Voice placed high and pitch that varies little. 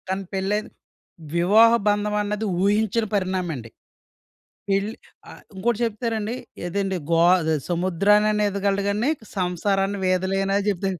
Yes: high, 200 Hz; narrow, 1.9 semitones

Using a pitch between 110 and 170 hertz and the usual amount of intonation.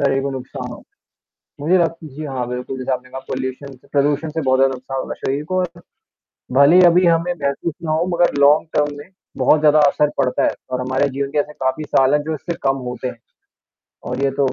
Yes: medium, 140 Hz; average, 3.1 semitones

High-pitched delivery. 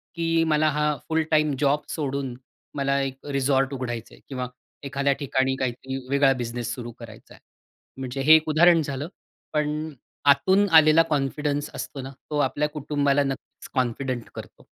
No: medium, 140 Hz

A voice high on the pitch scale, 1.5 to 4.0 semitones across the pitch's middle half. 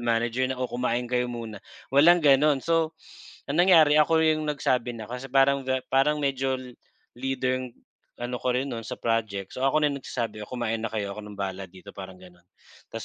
No: low, 125 Hz; average, 3.5 semitones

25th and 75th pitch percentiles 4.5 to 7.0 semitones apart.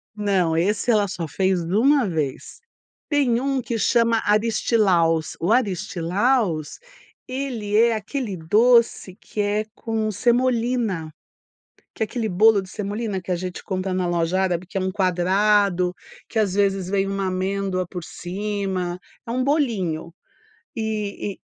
No: average, 3.6 semitones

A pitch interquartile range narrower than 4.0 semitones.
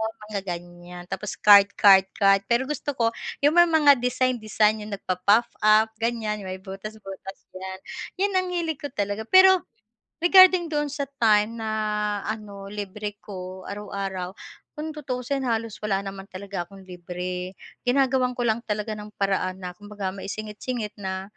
No: average, 4.3 semitones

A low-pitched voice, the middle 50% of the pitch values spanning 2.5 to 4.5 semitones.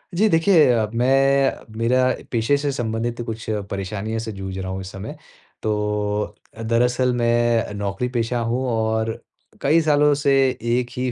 Yes: low, 120 Hz; average, 2.8 semitones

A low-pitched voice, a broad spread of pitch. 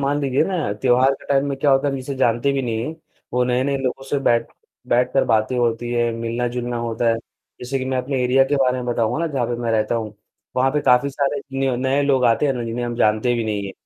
No: low, 125 Hz; narrow, 2.5 semitones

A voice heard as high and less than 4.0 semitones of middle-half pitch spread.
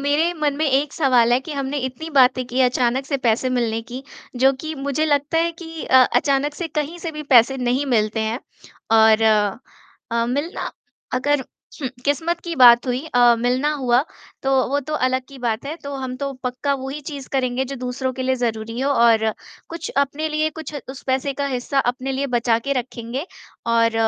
Yes: very high, 265 Hz; average, 2.9 semitones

